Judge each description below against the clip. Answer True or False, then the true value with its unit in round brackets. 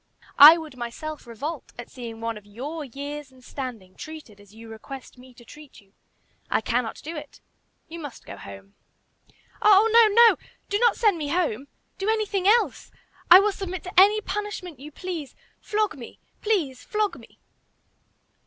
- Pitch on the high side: True (300 Hz)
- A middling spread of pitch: False (8.3 semitones)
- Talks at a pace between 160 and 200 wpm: True (170 wpm)